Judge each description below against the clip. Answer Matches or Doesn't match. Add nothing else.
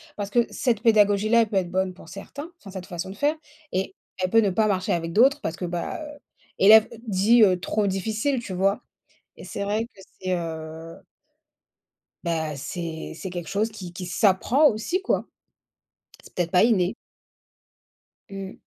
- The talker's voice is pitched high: Matches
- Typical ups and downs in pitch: Matches